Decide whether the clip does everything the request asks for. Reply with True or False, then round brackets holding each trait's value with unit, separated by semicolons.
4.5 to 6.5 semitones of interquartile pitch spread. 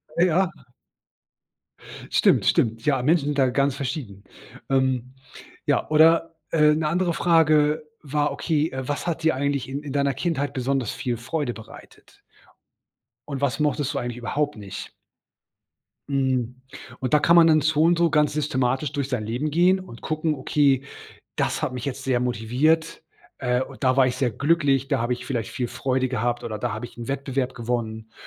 False (3.5 semitones)